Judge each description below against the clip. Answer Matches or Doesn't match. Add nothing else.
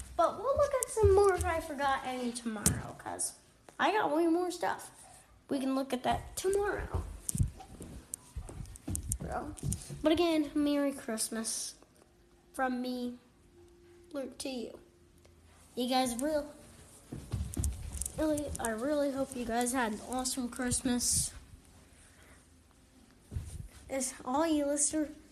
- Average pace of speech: Doesn't match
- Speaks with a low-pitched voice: Doesn't match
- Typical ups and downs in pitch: Matches